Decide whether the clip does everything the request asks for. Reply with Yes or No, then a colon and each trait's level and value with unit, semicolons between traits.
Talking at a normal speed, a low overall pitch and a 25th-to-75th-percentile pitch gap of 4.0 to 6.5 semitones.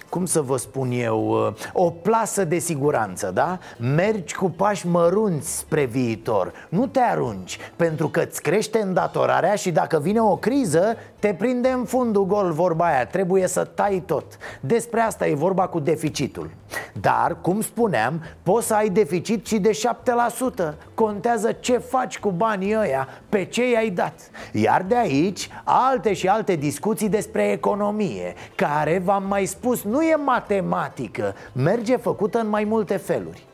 No: average, 155 wpm; high, 200 Hz; average, 4.7 semitones